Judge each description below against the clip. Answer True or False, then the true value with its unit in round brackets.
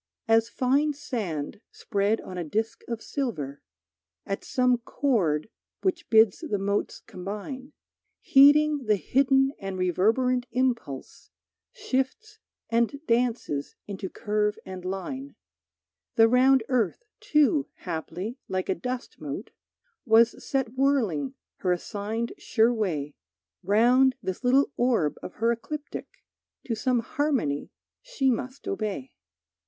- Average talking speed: False (120 wpm)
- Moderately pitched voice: False (230 Hz)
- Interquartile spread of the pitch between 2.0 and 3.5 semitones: False (5.3 semitones)